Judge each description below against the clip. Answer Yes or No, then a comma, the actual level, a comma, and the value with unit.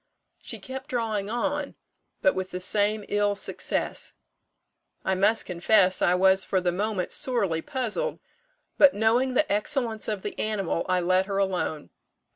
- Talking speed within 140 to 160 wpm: Yes, average, 150 wpm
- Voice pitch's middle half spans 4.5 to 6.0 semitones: No, average, 3.9 semitones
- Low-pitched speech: No, high, 205 Hz